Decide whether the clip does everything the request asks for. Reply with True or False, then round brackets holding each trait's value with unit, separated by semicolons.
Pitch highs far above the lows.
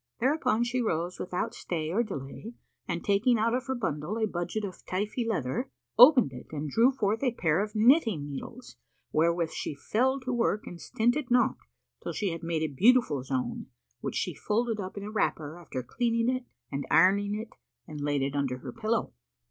True (7.0 semitones)